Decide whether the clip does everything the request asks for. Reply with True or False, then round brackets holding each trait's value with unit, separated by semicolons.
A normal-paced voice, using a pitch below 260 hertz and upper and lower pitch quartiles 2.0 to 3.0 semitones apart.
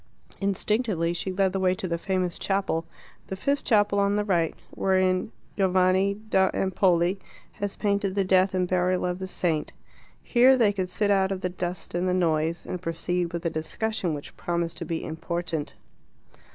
True (180 wpm; 185 Hz; 2.4 semitones)